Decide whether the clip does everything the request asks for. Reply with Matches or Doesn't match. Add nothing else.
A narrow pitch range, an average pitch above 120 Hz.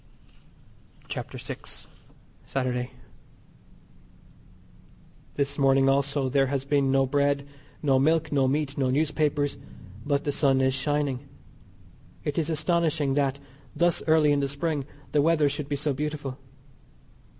Matches